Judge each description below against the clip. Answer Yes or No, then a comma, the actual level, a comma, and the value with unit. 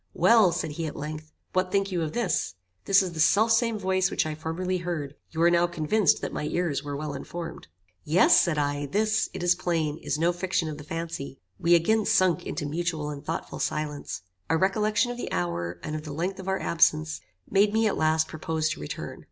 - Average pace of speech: No, fast, 215 wpm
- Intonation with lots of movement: No, average, 3.7 semitones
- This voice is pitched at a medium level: Yes, medium, 165 Hz